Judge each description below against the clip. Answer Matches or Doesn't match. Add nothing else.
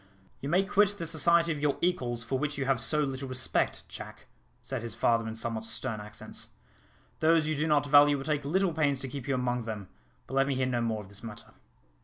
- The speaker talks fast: Matches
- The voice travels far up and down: Doesn't match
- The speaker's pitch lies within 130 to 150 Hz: Matches